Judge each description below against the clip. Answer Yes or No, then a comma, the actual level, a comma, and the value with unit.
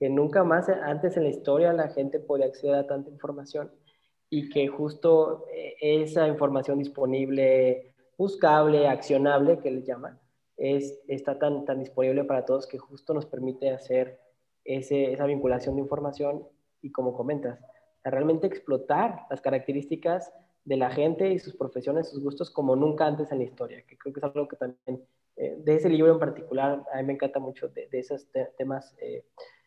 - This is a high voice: No, medium, 140 Hz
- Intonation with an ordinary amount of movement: Yes, average, 3.0 semitones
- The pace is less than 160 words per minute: No, average, 180 wpm